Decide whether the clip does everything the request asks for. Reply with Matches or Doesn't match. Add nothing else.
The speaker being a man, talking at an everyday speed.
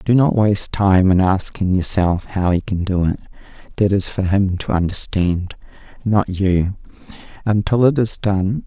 Matches